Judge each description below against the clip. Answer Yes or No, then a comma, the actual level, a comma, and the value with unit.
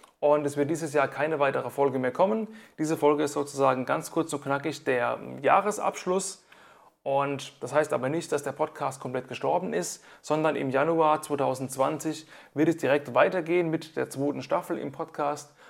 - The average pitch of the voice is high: No, medium, 150 Hz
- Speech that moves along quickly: No, average, 170 wpm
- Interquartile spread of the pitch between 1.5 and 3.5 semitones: Yes, average, 2.8 semitones